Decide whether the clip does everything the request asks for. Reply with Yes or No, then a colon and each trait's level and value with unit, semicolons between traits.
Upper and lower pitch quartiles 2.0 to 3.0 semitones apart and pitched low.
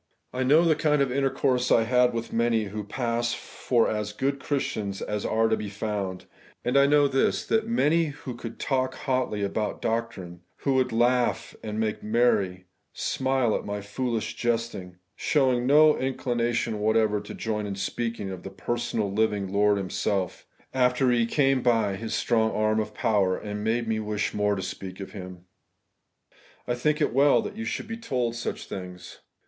No: average, 3.8 semitones; low, 115 Hz